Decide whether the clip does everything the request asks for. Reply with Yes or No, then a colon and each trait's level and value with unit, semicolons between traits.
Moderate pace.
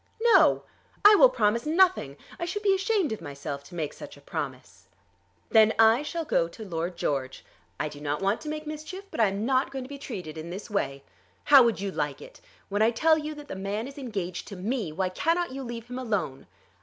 No: fast, 225 wpm